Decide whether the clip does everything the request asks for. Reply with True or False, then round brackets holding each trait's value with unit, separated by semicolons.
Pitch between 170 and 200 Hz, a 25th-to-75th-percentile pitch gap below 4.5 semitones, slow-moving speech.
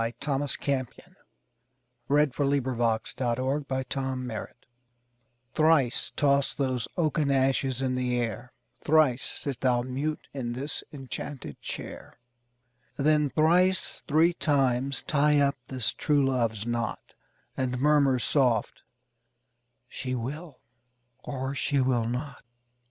False (135 Hz; 2.6 semitones; 120 wpm)